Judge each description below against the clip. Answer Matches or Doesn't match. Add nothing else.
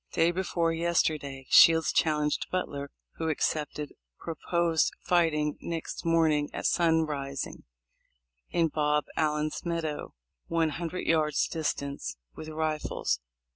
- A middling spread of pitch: Doesn't match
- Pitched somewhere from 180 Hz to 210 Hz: Doesn't match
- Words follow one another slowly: Matches